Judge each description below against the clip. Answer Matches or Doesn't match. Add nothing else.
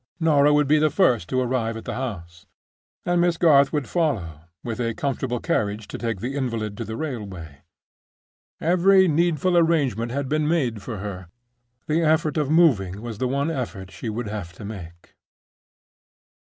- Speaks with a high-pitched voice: Doesn't match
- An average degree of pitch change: Doesn't match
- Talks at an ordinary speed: Matches